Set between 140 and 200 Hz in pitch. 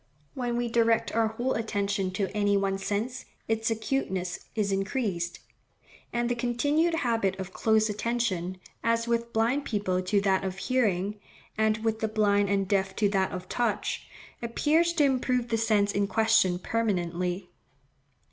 No: high, 215 Hz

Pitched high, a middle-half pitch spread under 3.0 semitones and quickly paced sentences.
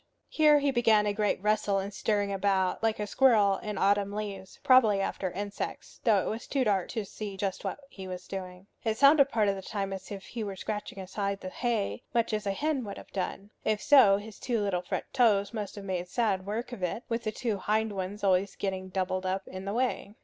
Yes: high, 205 Hz; narrow, 2.5 semitones; fast, 230 wpm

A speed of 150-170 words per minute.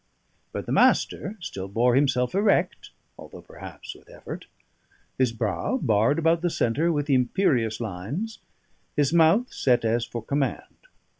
No: average, 140 wpm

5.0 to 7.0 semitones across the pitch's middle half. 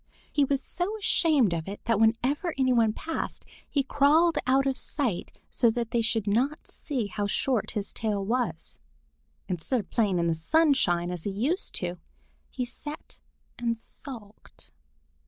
Yes: wide, 5.6 semitones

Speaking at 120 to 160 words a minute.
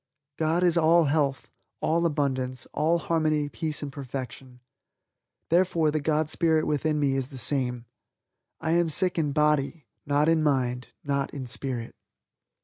Yes: average, 145 wpm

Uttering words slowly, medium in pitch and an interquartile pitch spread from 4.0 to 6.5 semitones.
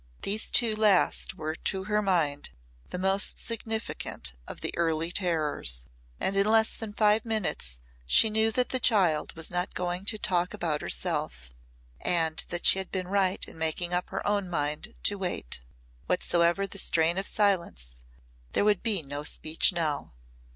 No: average, 165 wpm; medium, 180 Hz; average, 4.4 semitones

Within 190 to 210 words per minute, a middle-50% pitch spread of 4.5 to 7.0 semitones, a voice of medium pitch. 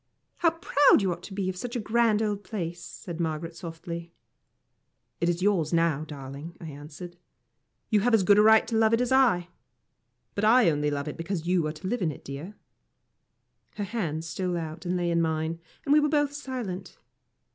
Yes: average, 200 wpm; average, 5.1 semitones; medium, 180 Hz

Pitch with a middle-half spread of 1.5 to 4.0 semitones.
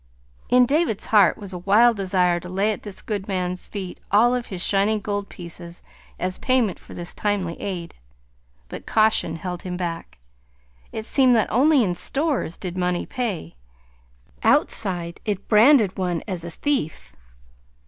Yes: average, 3.7 semitones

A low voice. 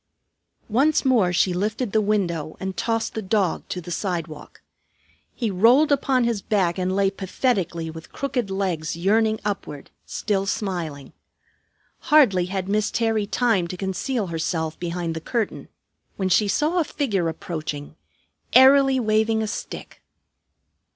No: high, 195 Hz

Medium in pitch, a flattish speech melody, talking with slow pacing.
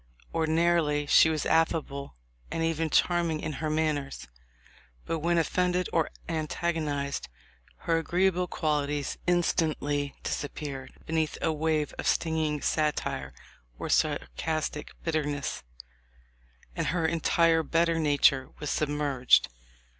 Yes: medium, 155 Hz; narrow, 1.9 semitones; slow, 115 wpm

